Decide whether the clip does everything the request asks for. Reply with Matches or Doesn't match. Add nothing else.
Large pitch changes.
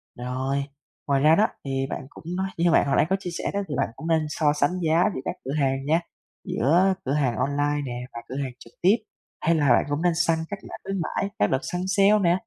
Doesn't match